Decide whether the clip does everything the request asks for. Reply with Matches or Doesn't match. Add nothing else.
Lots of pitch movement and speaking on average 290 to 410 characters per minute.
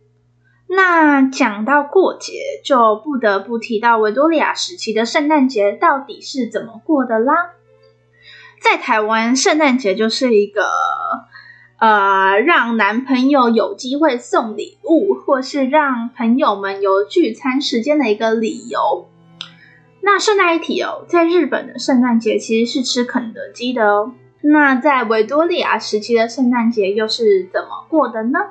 Doesn't match